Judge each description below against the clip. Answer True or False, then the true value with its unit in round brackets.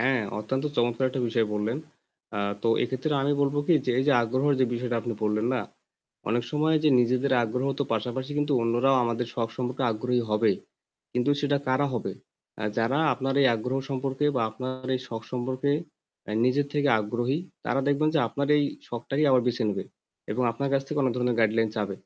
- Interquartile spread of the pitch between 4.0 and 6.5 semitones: False (2.8 semitones)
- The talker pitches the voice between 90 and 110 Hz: False (125 Hz)